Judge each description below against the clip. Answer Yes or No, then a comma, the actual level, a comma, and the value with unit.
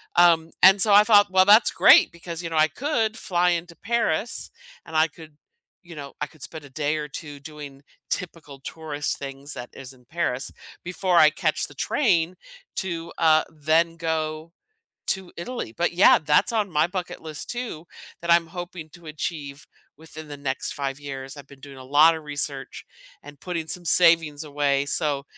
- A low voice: No, medium, 160 Hz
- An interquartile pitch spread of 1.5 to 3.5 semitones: Yes, average, 3.2 semitones